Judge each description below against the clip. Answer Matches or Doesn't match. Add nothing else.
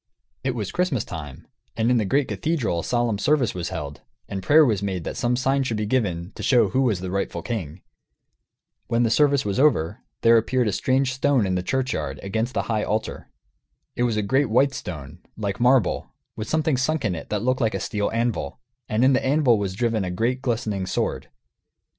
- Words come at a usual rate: Doesn't match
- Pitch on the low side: Matches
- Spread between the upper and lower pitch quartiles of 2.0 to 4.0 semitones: Doesn't match